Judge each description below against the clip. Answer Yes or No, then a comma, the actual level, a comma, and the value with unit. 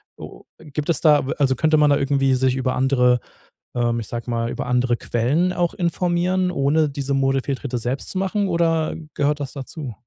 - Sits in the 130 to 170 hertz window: Yes, medium, 140 Hz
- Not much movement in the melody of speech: No, average, 4.1 semitones